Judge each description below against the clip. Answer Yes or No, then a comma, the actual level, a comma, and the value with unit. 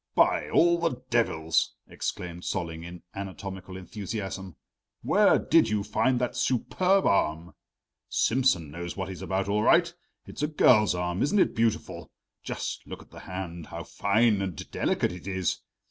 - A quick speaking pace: No, average, 155 wpm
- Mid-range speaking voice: No, very low, 95 Hz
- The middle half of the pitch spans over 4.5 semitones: Yes, average, 5.3 semitones